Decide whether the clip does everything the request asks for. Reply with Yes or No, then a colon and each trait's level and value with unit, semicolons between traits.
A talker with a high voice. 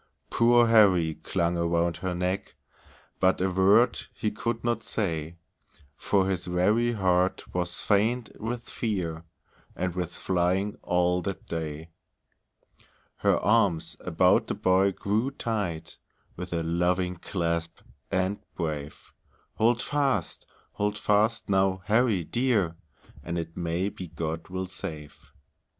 No: very low, 95 Hz